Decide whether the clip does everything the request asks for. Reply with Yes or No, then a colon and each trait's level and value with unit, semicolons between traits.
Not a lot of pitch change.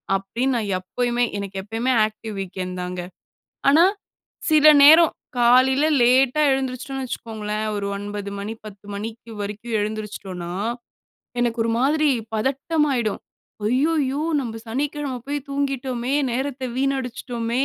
No: average, 4.2 semitones